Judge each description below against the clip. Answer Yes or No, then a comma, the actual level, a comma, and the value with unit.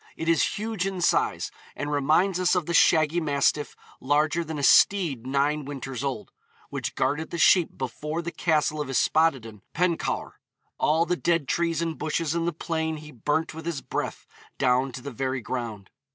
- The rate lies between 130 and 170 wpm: No, average, 180 wpm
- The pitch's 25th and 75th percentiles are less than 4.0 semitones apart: Yes, average, 3.5 semitones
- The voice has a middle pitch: Yes, medium, 155 Hz